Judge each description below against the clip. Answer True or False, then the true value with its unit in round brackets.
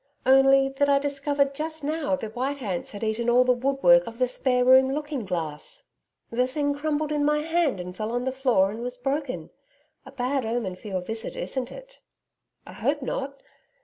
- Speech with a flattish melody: False (3.7 semitones)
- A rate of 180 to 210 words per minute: True (195 wpm)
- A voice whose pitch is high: True (265 Hz)